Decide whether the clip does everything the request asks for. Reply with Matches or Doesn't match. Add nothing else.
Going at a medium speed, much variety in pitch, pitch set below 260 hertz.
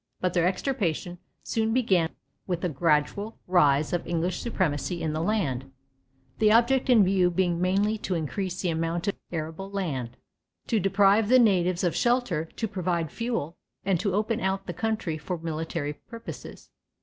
Doesn't match